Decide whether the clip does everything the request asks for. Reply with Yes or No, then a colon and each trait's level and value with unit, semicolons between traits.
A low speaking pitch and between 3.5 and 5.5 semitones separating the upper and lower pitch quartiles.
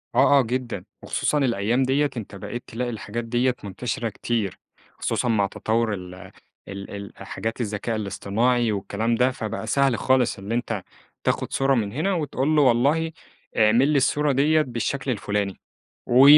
Yes: low, 120 Hz; average, 4.2 semitones